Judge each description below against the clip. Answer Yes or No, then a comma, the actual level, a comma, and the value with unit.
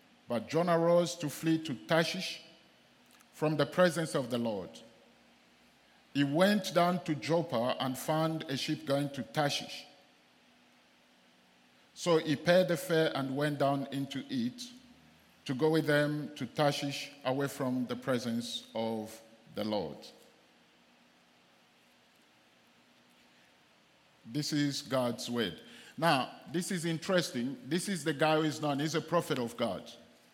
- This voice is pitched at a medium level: Yes, medium, 150 Hz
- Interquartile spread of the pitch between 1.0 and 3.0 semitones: No, average, 4.3 semitones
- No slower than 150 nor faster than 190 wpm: No, slow, 135 wpm